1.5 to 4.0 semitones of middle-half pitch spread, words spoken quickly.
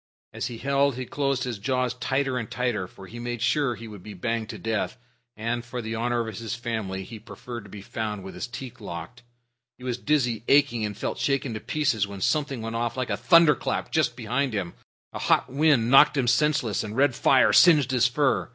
Yes: average, 3.3 semitones; fast, 215 wpm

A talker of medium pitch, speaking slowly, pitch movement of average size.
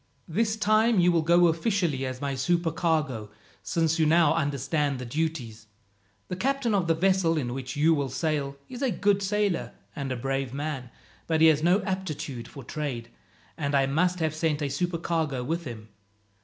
No: medium, 160 Hz; average, 180 wpm; average, 4.3 semitones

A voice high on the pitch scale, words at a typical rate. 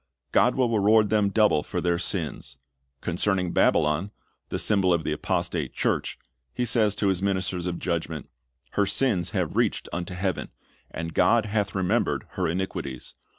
No: very low, 95 Hz; average, 155 wpm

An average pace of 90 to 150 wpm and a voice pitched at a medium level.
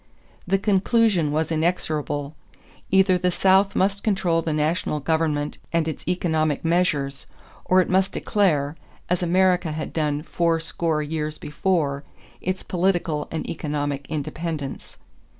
Yes: slow, 135 wpm; medium, 165 Hz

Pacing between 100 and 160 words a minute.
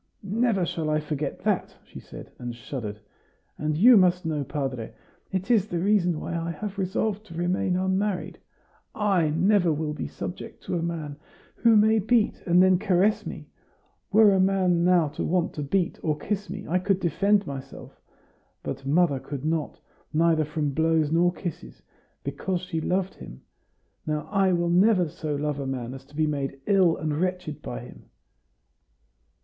No: average, 175 wpm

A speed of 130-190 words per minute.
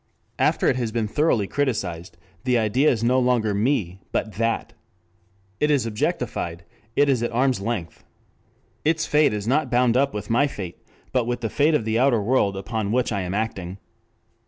Yes: average, 180 wpm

